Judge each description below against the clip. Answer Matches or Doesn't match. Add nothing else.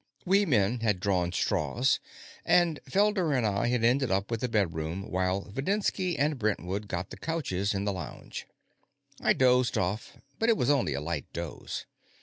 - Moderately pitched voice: Doesn't match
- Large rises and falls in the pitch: Matches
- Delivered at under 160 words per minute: Doesn't match